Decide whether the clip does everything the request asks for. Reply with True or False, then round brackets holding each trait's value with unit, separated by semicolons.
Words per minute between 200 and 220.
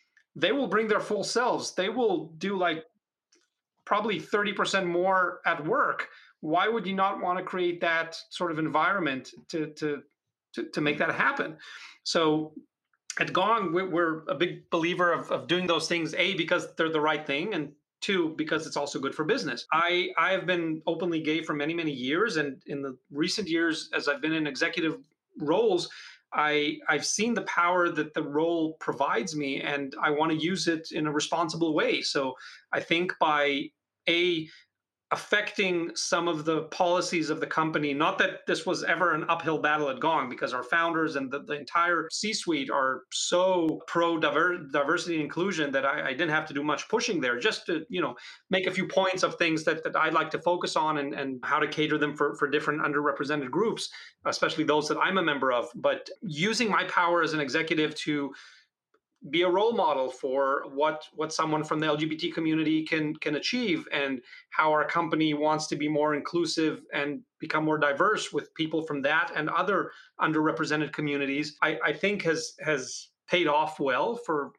False (190 wpm)